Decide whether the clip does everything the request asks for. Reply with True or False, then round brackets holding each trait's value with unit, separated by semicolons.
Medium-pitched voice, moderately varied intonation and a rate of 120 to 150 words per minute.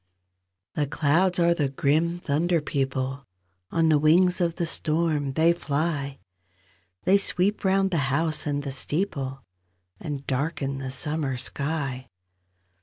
True (150 Hz; 3.6 semitones; 135 wpm)